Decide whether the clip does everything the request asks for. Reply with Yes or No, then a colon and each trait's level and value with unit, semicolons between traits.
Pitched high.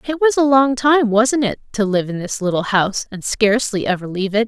Yes: high, 225 Hz